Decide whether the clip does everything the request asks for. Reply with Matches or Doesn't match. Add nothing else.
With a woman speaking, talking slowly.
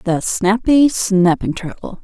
Matches